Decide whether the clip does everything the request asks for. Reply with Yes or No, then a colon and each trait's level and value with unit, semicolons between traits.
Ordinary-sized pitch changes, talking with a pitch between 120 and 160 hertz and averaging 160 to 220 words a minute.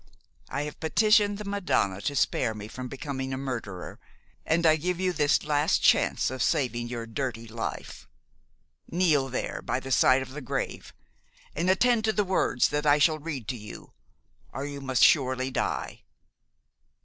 Yes: average, 4.4 semitones; medium, 140 Hz; average, 170 wpm